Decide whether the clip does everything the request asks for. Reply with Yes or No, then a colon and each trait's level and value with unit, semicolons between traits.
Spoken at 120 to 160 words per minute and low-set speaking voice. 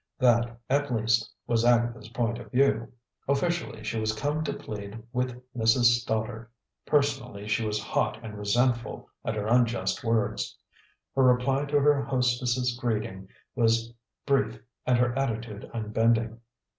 Yes: average, 140 wpm; low, 120 Hz